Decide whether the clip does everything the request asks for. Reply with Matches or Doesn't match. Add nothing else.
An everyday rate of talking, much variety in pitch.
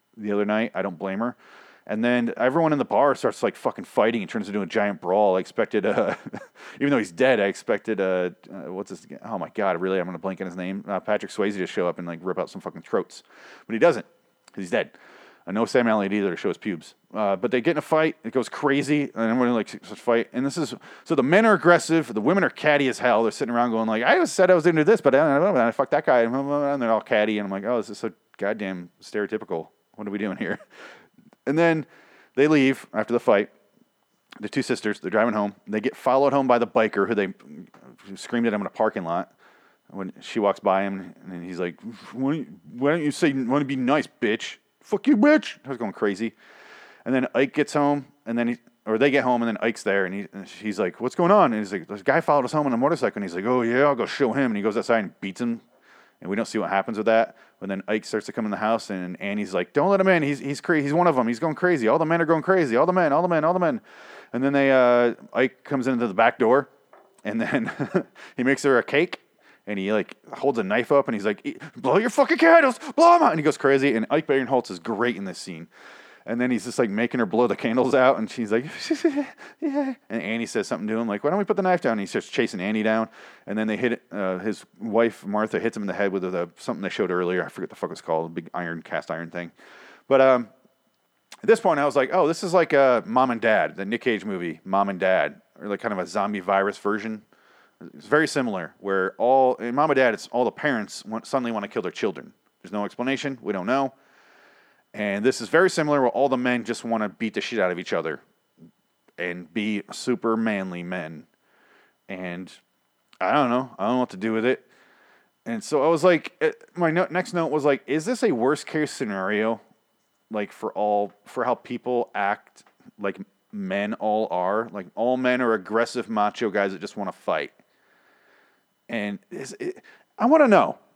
Doesn't match